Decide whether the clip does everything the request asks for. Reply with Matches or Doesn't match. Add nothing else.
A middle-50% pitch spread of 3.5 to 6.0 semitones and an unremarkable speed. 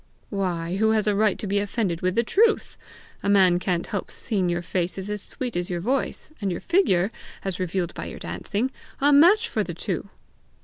Doesn't match